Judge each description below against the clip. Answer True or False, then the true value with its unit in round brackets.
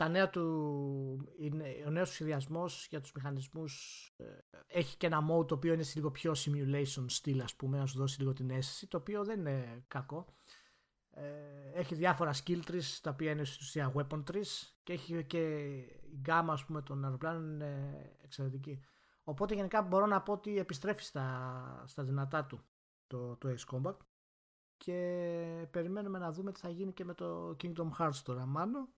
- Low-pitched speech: False (155 Hz)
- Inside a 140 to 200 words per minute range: True (170 wpm)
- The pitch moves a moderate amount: True (4.1 semitones)